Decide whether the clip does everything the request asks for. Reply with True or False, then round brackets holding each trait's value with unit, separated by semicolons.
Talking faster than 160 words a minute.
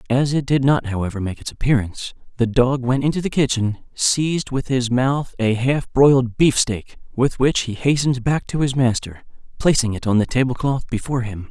True (200 wpm)